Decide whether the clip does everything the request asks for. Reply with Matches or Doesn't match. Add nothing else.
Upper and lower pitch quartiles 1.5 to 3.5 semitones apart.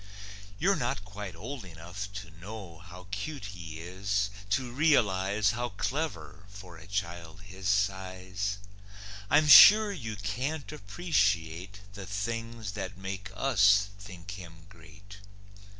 Matches